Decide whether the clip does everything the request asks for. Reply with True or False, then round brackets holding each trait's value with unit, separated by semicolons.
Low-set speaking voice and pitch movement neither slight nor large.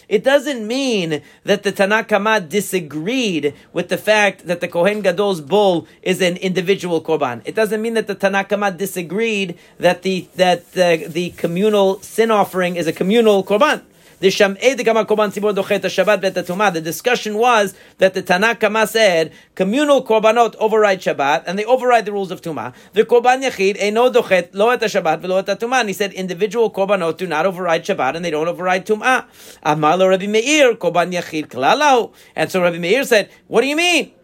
False (195 Hz; 3.6 semitones)